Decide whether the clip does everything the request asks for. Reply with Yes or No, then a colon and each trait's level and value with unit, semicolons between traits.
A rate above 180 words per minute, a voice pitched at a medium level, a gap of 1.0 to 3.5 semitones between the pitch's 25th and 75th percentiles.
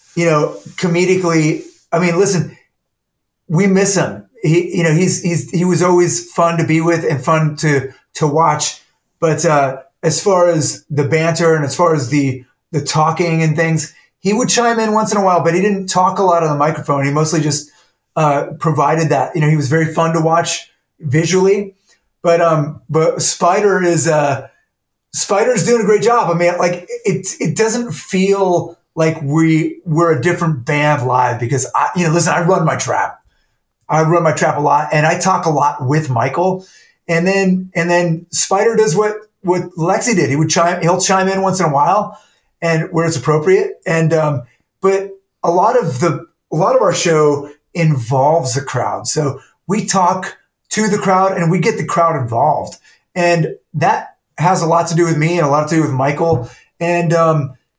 Yes: average, 195 wpm; medium, 165 Hz; average, 2.9 semitones